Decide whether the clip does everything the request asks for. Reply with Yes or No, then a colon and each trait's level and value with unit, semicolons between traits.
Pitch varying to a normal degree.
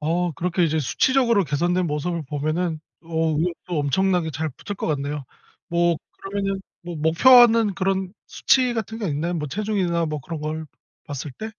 Yes: average, 4.0 semitones